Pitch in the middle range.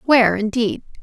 No: high, 230 Hz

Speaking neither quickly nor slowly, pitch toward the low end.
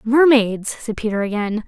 No: average, 145 wpm; high, 225 Hz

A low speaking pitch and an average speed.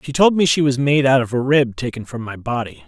No: low, 130 Hz; fast, 290 wpm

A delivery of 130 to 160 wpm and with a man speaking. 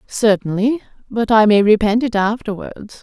No: average, 140 wpm; female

